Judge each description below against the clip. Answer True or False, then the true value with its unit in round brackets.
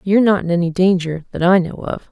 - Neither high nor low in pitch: True (180 Hz)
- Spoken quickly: True (255 wpm)